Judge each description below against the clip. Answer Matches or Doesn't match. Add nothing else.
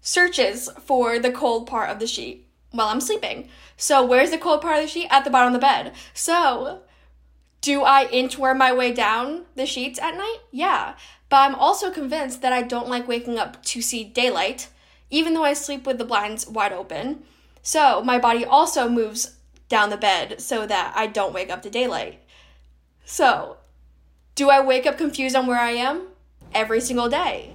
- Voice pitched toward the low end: Doesn't match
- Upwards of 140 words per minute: Matches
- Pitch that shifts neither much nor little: Matches